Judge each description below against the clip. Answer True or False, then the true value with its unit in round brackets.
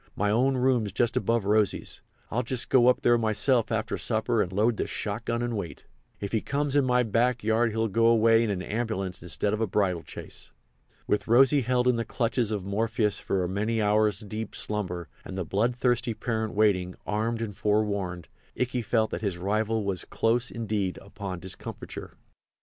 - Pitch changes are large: False (2.6 semitones)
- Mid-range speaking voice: False (110 Hz)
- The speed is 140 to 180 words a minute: False (190 wpm)